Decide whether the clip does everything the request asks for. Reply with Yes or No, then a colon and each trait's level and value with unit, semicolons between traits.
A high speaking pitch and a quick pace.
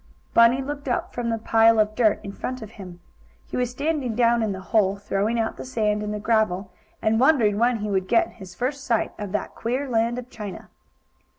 Yes: high, 225 Hz; fast, 215 wpm